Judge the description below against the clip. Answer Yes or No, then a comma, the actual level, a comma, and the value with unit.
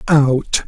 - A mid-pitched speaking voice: Yes, medium, 145 Hz